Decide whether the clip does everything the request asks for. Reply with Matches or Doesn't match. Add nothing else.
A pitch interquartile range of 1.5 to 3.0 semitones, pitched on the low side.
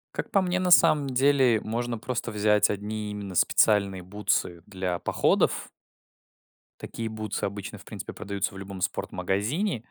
Doesn't match